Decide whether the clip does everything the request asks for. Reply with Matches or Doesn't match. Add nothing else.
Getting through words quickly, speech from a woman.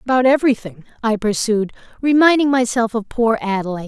Doesn't match